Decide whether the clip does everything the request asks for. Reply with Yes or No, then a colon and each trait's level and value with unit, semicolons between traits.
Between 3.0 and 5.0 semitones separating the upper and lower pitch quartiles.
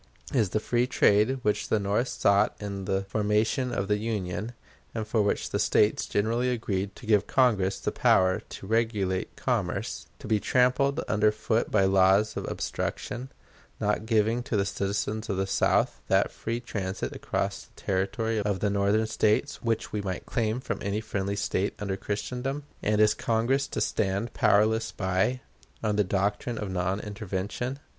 No: narrow, 2.4 semitones